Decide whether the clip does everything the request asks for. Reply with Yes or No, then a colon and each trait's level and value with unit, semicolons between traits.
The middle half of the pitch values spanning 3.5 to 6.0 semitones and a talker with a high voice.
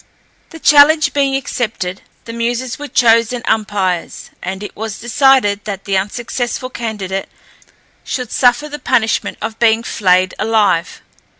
Yes: average, 3.9 semitones; high, 225 Hz